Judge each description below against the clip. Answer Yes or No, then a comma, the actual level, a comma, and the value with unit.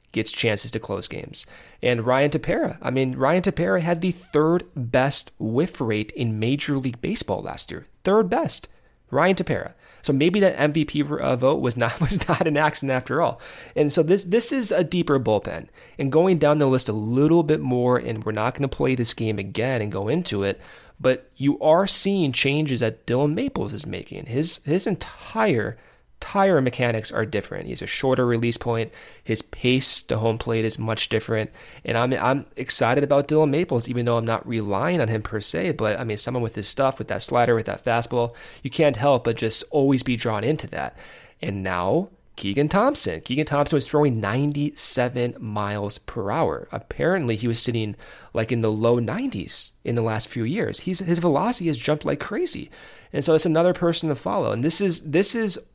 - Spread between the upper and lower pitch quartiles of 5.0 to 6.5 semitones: Yes, average, 5.3 semitones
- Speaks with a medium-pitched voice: No, low, 130 Hz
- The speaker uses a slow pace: No, average, 200 wpm